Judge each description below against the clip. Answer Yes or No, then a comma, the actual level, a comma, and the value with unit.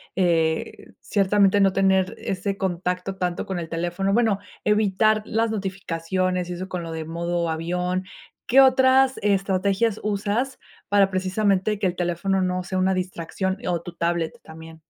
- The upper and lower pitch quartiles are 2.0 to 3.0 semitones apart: Yes, narrow, 2.5 semitones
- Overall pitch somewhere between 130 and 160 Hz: No, medium, 185 Hz